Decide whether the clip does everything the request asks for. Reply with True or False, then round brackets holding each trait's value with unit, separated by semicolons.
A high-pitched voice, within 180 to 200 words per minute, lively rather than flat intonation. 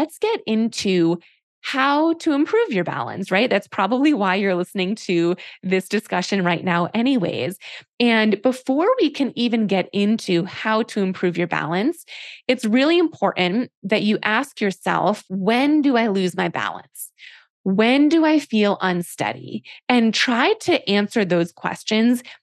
False (220 Hz; 150 wpm; 5.8 semitones)